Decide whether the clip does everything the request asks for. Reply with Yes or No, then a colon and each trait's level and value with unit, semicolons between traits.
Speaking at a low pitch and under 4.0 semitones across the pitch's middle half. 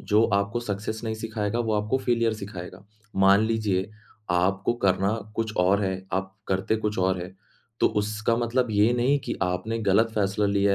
Yes: low, 105 Hz; narrow, 2.6 semitones